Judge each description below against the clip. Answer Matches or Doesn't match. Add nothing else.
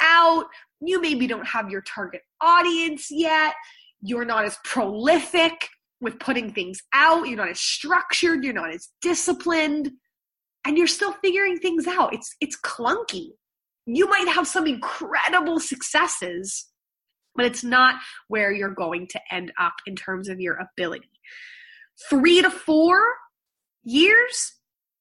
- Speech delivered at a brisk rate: Doesn't match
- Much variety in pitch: Matches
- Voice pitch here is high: Matches